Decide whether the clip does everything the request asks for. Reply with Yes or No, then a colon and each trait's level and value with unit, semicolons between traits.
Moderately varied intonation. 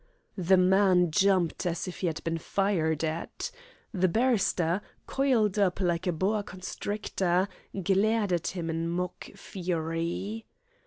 Yes: average, 3.0 semitones